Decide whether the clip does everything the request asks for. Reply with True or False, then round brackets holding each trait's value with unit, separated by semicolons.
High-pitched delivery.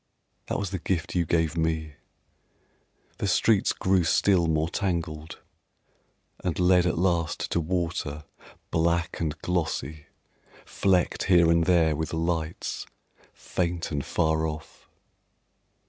False (85 Hz)